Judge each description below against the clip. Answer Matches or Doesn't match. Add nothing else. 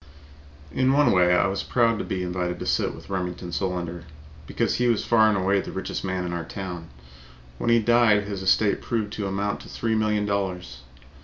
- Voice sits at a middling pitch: Doesn't match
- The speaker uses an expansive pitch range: Doesn't match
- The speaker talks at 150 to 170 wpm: Doesn't match